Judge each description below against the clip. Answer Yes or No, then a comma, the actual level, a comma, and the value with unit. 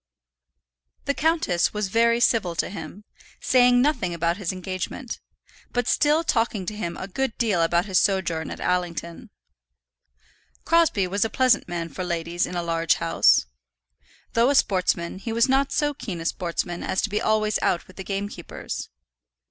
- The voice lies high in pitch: Yes, high, 195 Hz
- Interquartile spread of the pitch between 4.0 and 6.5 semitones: Yes, average, 5.1 semitones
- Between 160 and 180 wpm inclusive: Yes, average, 165 wpm